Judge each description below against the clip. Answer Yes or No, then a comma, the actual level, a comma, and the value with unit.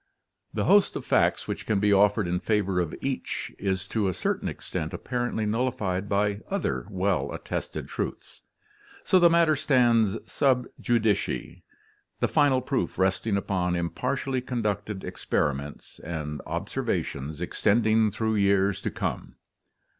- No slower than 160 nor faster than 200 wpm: No, average, 140 wpm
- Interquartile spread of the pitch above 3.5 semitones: Yes, average, 4.5 semitones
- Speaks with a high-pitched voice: No, low, 105 Hz